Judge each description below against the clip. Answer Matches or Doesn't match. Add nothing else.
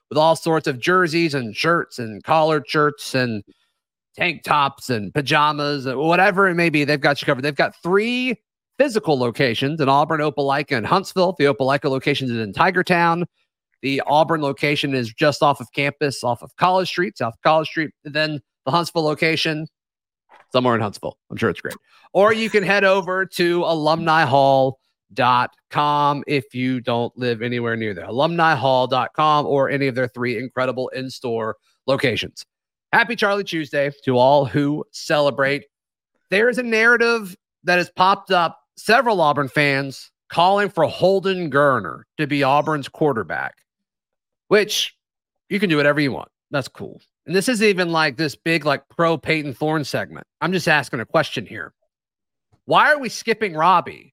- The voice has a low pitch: Doesn't match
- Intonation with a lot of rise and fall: Doesn't match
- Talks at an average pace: Matches